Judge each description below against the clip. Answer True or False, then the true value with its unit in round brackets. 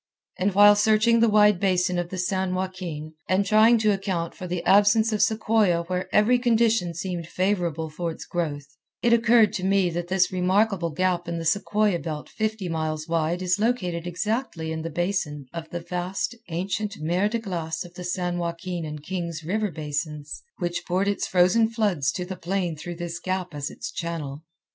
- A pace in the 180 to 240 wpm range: True (185 wpm)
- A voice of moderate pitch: True (180 Hz)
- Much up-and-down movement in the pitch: False (3.5 semitones)